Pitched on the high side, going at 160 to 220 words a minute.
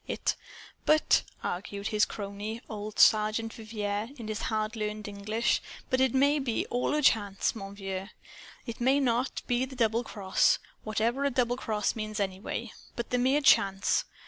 Yes: high, 220 Hz; average, 170 wpm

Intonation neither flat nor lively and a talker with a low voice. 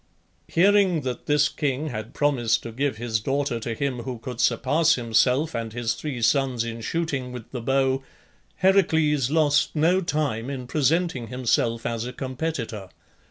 Yes: average, 4.3 semitones; low, 130 Hz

